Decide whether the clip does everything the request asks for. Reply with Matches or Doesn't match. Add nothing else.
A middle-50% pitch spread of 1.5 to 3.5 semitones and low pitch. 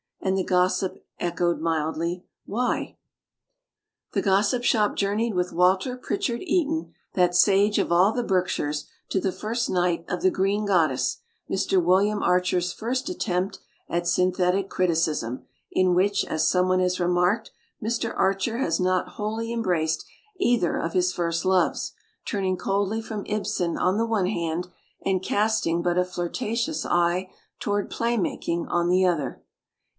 Doesn't match